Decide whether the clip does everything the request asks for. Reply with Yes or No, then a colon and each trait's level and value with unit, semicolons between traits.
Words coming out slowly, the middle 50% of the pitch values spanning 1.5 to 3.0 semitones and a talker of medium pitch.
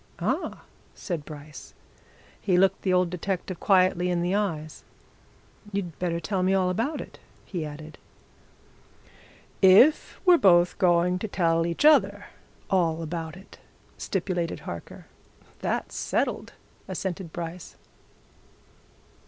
Yes: slow, 120 wpm; narrow, 2.4 semitones; medium, 180 Hz